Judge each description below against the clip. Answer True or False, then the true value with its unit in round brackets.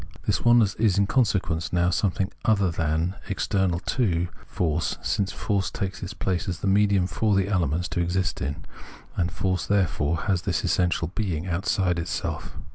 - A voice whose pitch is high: False (95 Hz)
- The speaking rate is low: False (170 wpm)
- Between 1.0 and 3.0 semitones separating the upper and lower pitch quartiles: True (2.6 semitones)